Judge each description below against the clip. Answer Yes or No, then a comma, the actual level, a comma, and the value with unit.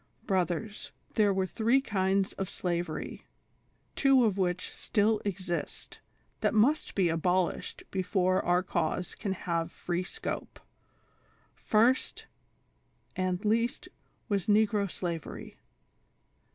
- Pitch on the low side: No, high, 190 Hz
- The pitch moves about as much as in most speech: Yes, average, 3.2 semitones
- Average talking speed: No, slow, 110 wpm